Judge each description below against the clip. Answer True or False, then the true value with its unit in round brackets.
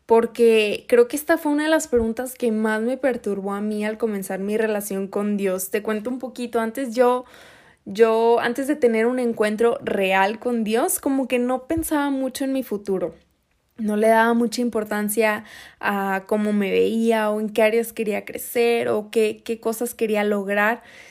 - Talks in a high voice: True (225 Hz)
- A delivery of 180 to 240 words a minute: True (185 wpm)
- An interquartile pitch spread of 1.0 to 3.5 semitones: True (2.7 semitones)